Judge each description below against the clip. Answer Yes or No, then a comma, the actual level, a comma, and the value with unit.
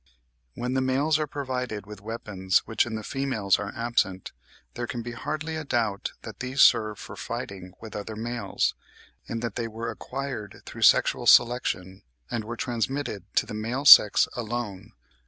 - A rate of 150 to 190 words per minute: Yes, average, 170 wpm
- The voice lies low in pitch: Yes, low, 115 Hz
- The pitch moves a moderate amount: Yes, average, 3.2 semitones